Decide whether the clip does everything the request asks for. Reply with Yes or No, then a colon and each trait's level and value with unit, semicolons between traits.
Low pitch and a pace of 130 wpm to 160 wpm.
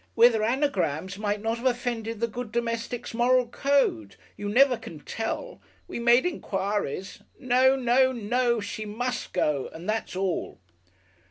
No: high, 230 Hz; average, 150 wpm